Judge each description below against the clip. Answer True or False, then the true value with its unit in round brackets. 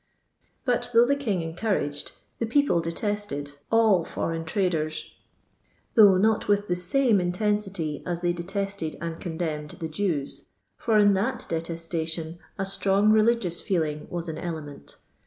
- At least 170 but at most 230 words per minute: False (150 wpm)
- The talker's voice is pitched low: False (180 Hz)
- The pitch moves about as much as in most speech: True (4.2 semitones)